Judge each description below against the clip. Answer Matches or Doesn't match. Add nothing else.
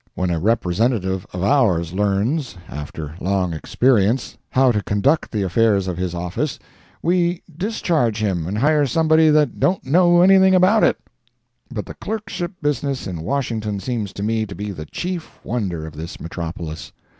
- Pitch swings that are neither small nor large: Doesn't match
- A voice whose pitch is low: Matches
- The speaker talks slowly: Doesn't match